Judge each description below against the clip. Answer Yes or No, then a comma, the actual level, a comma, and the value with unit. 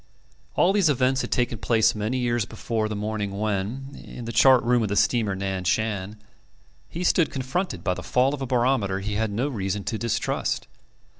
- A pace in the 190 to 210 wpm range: Yes, average, 195 wpm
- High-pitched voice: No, low, 115 Hz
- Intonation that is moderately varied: Yes, average, 3.9 semitones